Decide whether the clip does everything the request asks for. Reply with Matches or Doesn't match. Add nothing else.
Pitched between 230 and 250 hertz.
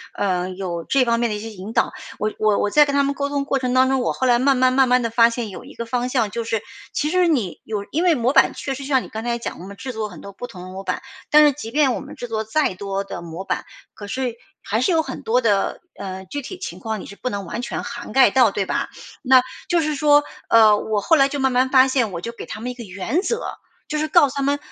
Matches